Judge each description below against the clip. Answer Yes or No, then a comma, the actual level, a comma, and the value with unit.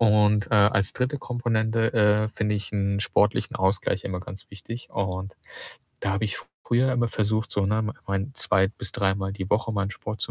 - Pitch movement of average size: No, narrow, 2.0 semitones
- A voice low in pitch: Yes, low, 105 Hz